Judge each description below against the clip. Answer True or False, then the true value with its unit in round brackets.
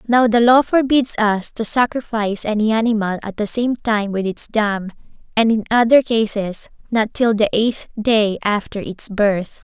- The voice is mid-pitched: False (220 Hz)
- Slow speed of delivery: False (175 wpm)